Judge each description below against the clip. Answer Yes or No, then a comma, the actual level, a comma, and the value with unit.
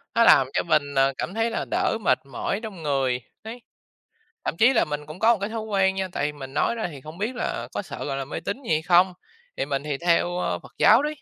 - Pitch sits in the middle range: Yes, medium, 180 Hz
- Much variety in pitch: Yes, wide, 7.3 semitones